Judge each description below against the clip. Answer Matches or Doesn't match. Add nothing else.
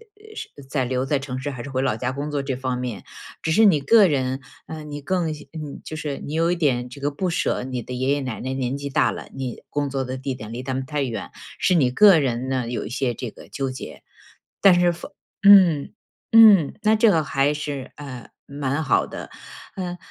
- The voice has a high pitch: Doesn't match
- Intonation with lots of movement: Doesn't match